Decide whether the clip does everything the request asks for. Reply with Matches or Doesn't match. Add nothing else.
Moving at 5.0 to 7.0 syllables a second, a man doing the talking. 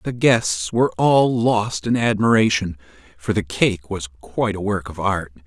Doesn't match